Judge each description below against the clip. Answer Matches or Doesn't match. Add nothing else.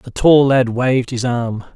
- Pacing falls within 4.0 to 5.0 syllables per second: Matches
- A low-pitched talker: Matches